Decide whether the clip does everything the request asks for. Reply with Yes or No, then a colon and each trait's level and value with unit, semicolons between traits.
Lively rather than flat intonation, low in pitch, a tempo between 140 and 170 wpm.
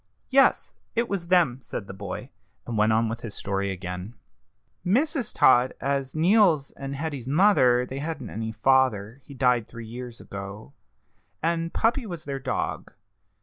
Yes: wide, 6.7 semitones; low, 130 Hz; average, 155 wpm